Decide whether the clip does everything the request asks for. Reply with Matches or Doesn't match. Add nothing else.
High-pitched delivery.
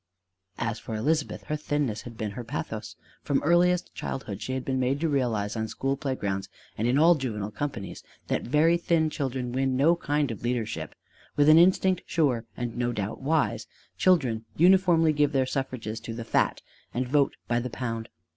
Doesn't match